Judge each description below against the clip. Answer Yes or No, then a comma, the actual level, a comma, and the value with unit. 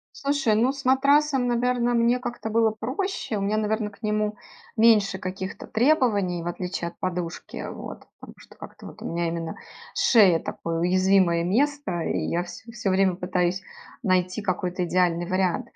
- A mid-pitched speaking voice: No, high, 200 Hz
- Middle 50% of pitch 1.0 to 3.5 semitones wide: No, average, 4.8 semitones